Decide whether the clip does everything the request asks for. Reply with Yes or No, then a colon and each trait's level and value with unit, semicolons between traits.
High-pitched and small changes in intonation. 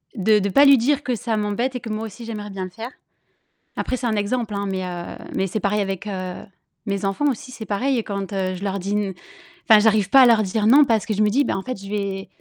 No: high, 210 Hz; average, 3.0 semitones